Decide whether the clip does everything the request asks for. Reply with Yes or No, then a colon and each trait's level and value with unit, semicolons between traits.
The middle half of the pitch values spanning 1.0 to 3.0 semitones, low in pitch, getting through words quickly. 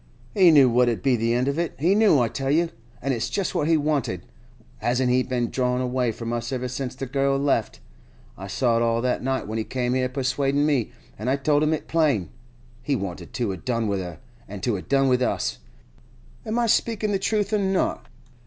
No: average, 3.7 semitones; low, 130 Hz; fast, 220 wpm